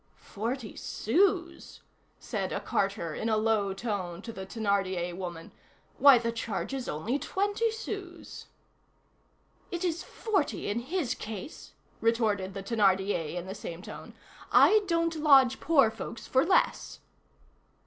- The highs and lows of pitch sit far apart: Yes, wide, 8.6 semitones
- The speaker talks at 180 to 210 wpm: No, slow, 135 wpm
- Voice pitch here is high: Yes, high, 230 Hz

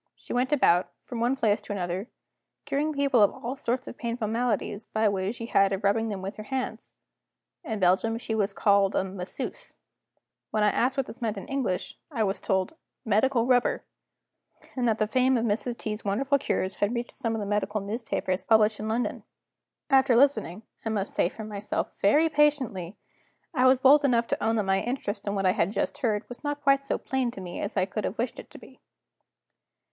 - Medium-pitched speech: No, high, 225 Hz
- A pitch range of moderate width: Yes, average, 4.0 semitones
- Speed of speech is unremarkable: No, fast, 210 wpm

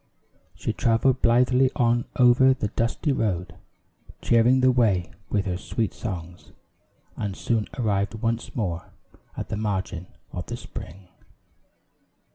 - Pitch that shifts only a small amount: No, average, 4.2 semitones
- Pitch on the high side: No, low, 110 Hz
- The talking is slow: Yes, slow, 125 wpm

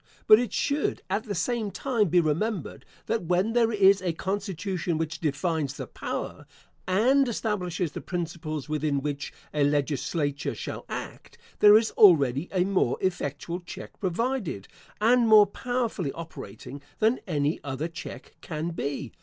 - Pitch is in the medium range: Yes, medium, 180 Hz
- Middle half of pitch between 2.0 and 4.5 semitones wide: No, wide, 5.6 semitones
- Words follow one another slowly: No, average, 145 wpm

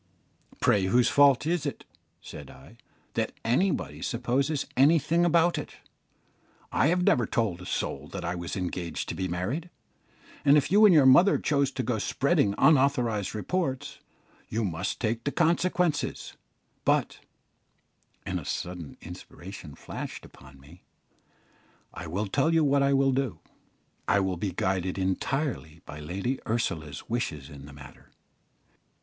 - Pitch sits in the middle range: No, low, 115 Hz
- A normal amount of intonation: No, wide, 8.1 semitones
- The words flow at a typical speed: Yes, average, 145 wpm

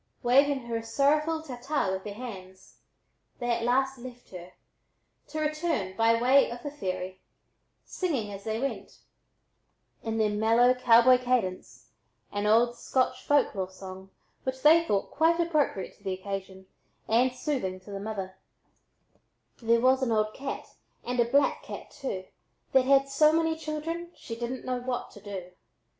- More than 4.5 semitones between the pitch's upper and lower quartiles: Yes, average, 5.2 semitones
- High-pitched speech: Yes, high, 240 Hz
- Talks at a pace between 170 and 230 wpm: No, average, 160 wpm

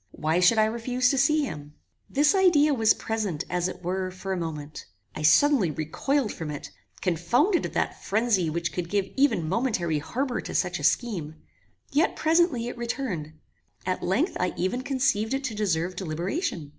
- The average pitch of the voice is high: Yes, high, 205 Hz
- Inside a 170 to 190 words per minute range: Yes, average, 175 wpm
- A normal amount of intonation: No, wide, 7.6 semitones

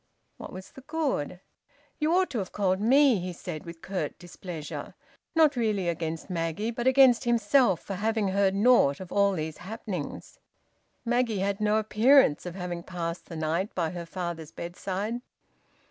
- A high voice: Yes, high, 195 Hz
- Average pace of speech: Yes, average, 160 wpm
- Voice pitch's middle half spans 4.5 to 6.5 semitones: Yes, average, 5.1 semitones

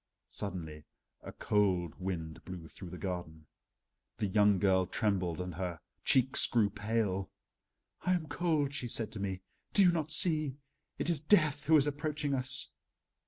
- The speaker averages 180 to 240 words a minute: No, average, 160 wpm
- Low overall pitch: Yes, low, 105 Hz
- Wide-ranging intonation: Yes, wide, 8.0 semitones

